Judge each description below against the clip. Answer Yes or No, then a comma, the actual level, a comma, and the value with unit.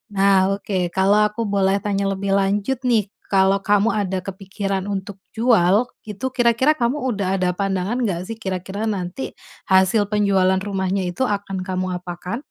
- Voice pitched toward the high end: Yes, high, 195 Hz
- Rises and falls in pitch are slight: Yes, narrow, 1.8 semitones